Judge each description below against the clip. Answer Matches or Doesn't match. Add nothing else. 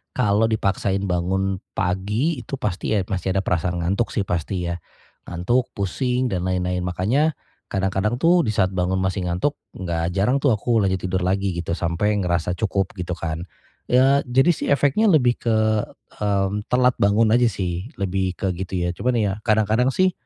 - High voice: Doesn't match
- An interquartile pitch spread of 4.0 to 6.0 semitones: Matches